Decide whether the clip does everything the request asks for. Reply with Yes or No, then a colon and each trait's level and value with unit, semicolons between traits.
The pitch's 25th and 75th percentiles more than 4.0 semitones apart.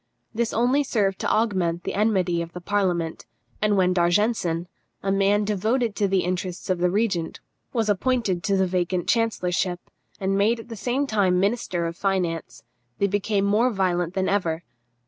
No: average, 3.2 semitones